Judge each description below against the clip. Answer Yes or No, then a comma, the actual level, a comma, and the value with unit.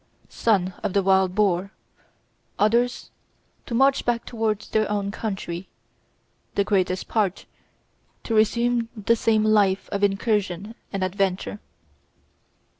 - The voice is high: Yes, high, 205 Hz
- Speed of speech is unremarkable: No, slow, 115 wpm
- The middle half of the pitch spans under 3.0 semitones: Yes, narrow, 2.6 semitones